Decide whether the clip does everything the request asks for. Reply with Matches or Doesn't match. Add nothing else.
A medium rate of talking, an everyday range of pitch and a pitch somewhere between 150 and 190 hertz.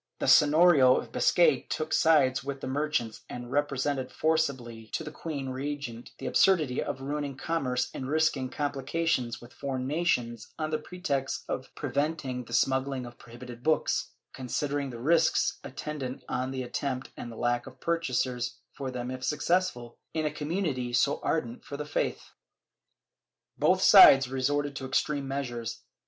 Doesn't match